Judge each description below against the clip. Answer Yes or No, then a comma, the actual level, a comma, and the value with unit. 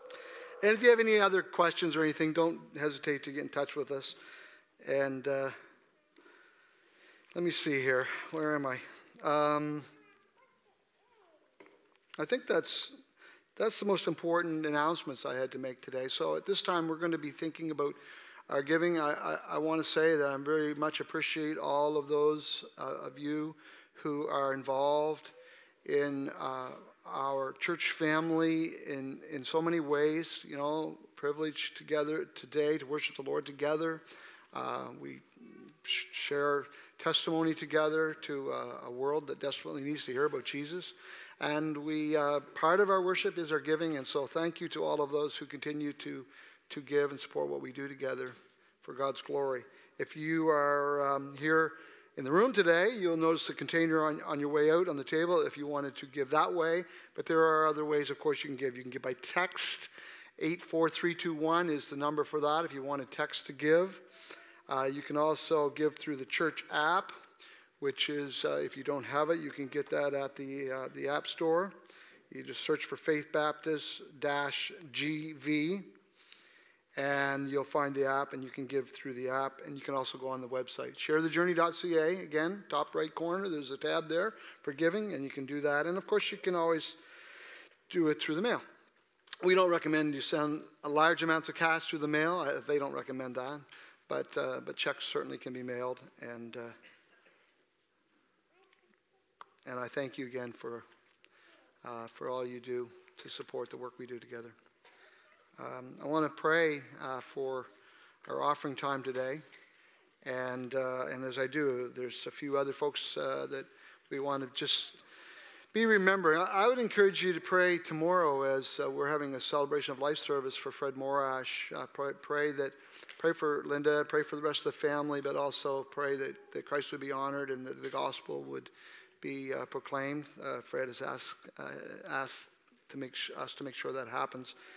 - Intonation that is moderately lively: Yes, average, 3.0 semitones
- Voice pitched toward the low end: No, medium, 150 Hz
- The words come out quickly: No, average, 185 wpm